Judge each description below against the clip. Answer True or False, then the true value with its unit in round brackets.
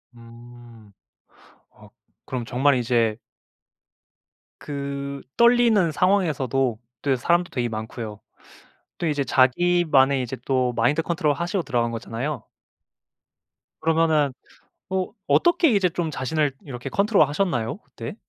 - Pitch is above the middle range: False (140 Hz)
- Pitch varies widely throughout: True (5.9 semitones)